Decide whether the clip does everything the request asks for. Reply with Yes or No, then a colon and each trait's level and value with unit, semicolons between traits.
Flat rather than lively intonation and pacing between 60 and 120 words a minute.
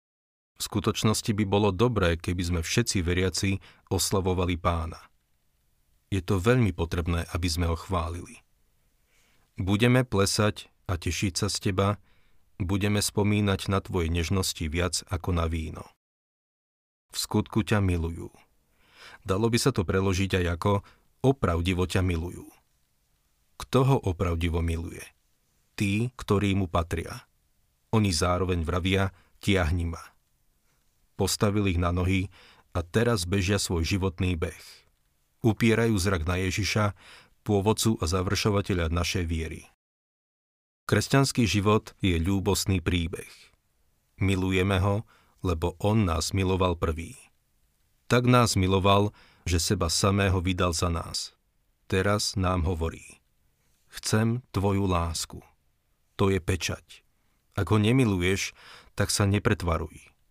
No: average, 3.4 semitones; average, 115 wpm